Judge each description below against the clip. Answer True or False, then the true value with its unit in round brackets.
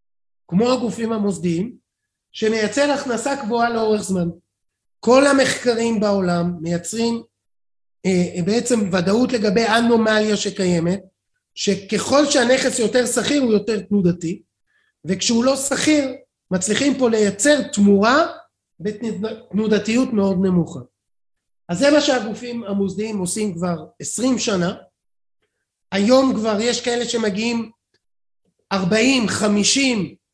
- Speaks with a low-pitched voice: False (220 Hz)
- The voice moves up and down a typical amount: True (4.2 semitones)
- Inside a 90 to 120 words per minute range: True (100 wpm)